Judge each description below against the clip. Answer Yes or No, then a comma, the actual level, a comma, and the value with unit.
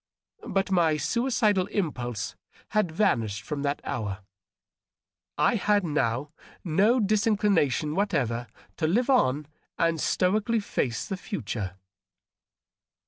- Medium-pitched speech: Yes, medium, 165 Hz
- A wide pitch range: Yes, wide, 8.4 semitones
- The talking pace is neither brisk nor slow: No, slow, 105 wpm